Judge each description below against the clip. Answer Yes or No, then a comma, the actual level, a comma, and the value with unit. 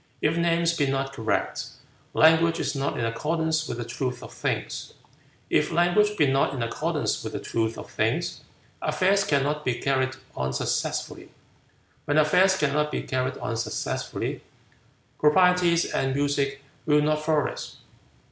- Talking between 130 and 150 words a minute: Yes, average, 145 wpm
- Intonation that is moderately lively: Yes, average, 3.9 semitones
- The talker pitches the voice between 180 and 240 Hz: No, medium, 150 Hz